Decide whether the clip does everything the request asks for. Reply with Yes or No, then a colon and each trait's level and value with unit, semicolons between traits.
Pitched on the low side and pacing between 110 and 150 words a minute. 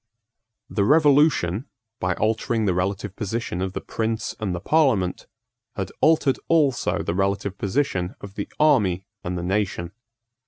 Yes: low, 100 Hz; average, 145 wpm